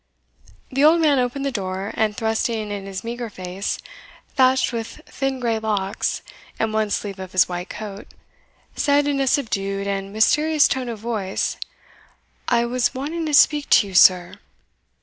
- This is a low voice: No, high, 225 Hz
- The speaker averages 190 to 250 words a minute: No, average, 165 wpm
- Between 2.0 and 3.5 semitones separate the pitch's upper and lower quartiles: No, average, 5.2 semitones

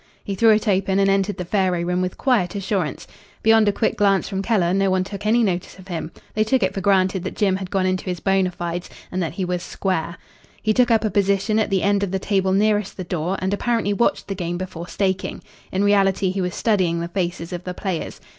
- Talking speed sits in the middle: No, fast, 240 wpm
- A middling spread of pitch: No, narrow, 2.0 semitones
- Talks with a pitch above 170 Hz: Yes, high, 190 Hz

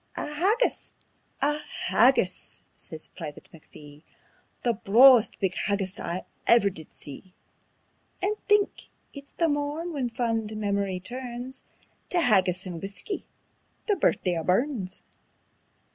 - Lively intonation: Yes, wide, 7.6 semitones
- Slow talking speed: Yes, slow, 120 wpm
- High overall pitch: Yes, high, 225 Hz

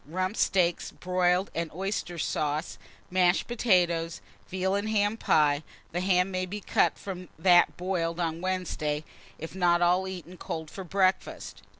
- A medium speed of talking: Yes, average, 145 wpm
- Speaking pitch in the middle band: Yes, medium, 180 Hz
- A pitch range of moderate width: No, narrow, 2.1 semitones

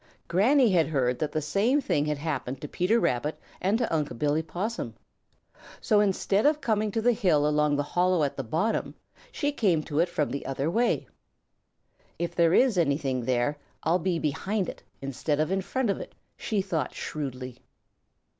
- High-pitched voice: No, medium, 165 Hz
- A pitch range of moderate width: No, wide, 6.0 semitones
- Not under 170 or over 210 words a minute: Yes, average, 185 wpm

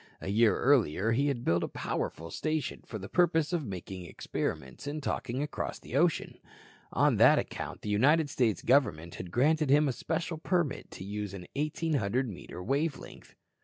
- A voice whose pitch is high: No, low, 130 Hz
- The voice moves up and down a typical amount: No, wide, 7.3 semitones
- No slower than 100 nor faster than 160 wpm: No, average, 175 wpm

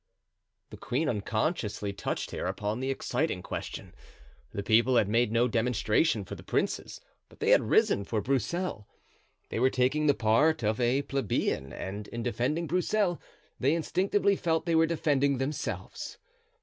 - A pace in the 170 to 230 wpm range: No, average, 155 wpm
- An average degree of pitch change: No, wide, 6.5 semitones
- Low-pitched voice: Yes, low, 125 Hz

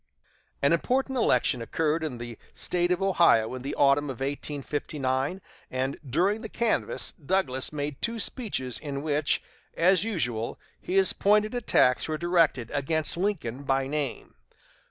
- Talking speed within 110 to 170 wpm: Yes, average, 140 wpm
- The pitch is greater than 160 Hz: No, medium, 150 Hz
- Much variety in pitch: Yes, wide, 5.8 semitones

